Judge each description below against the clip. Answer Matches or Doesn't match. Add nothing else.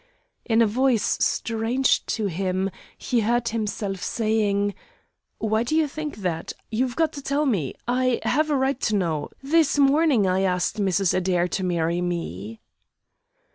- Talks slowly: Doesn't match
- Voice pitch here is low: Doesn't match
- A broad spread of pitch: Matches